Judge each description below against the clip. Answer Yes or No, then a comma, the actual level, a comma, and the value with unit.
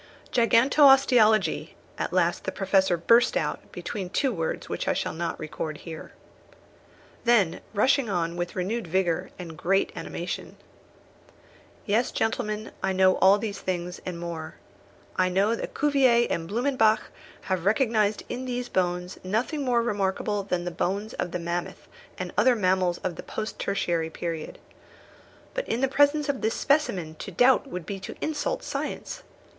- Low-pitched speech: No, high, 200 Hz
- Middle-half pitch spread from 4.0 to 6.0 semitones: Yes, average, 5.1 semitones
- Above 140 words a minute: Yes, average, 155 wpm